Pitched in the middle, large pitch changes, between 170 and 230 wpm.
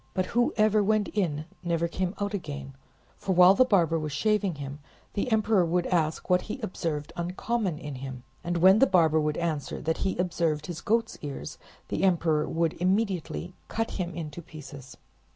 No: medium, 175 Hz; average, 4.2 semitones; average, 175 wpm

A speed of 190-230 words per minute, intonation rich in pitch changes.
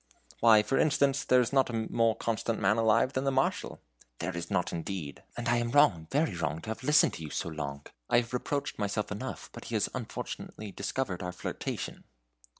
Yes: average, 200 wpm; wide, 6.3 semitones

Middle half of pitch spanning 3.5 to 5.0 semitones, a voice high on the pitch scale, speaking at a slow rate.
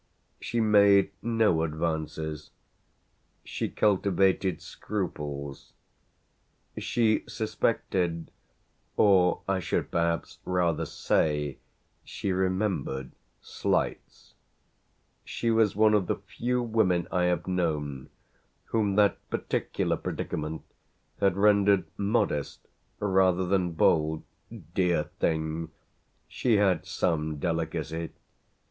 No: average, 4.1 semitones; very low, 90 Hz; slow, 90 wpm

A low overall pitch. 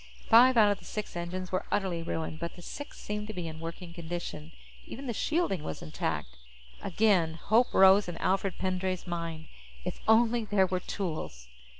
No: medium, 185 Hz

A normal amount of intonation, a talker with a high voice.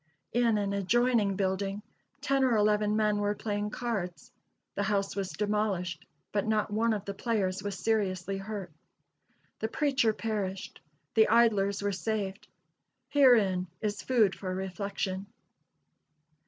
No: narrow, 2.1 semitones; high, 205 Hz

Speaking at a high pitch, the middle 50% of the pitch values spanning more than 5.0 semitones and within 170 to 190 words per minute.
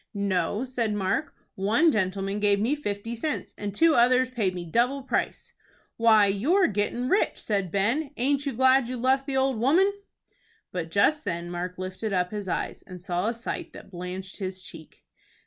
Yes: high, 215 Hz; wide, 5.5 semitones; average, 180 wpm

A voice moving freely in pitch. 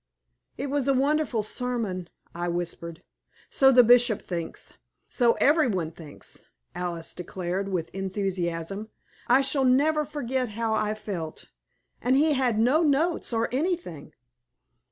Yes: wide, 6.9 semitones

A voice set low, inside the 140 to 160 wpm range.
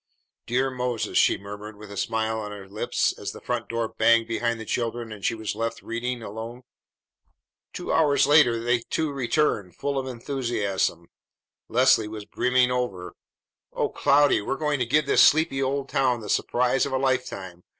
No: low, 120 Hz; average, 175 wpm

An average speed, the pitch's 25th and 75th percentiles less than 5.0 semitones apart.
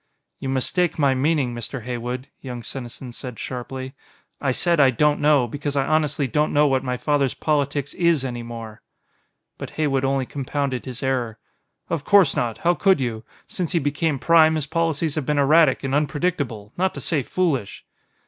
Yes: average, 175 wpm; average, 3.3 semitones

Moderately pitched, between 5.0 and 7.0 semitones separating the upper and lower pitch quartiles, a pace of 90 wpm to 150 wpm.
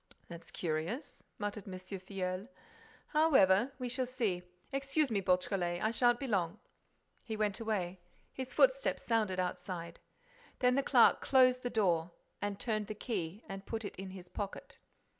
No: high, 205 Hz; average, 5.3 semitones; average, 145 wpm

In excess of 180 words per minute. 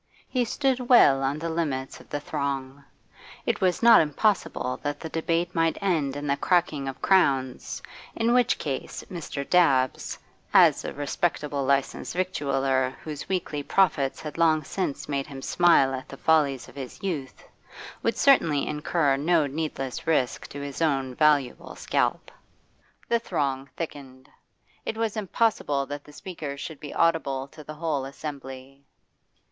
No: average, 150 wpm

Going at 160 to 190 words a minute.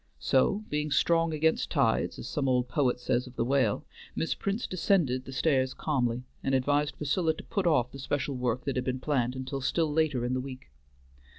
No: average, 200 wpm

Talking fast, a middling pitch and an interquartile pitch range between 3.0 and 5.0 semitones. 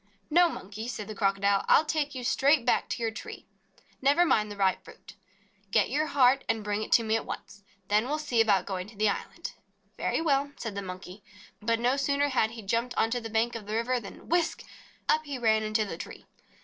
No: fast, 225 wpm; high, 225 Hz; average, 4.7 semitones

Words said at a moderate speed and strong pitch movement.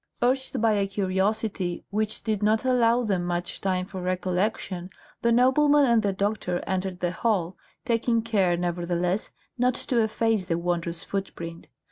No: average, 150 wpm; average, 4.2 semitones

